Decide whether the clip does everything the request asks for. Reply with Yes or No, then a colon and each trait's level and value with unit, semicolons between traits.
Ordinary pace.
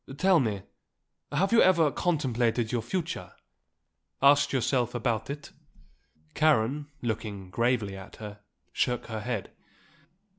No: slow, 115 wpm